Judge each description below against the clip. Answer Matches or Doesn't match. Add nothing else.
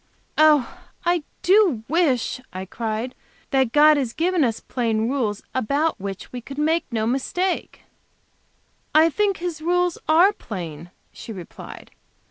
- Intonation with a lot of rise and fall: Matches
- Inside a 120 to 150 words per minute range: Matches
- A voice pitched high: Matches